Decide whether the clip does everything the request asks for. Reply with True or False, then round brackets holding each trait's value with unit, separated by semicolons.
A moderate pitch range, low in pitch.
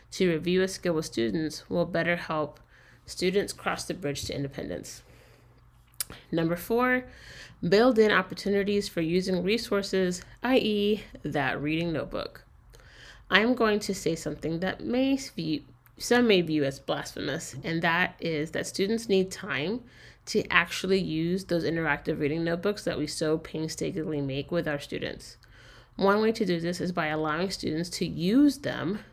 False (4.7 semitones; 170 Hz)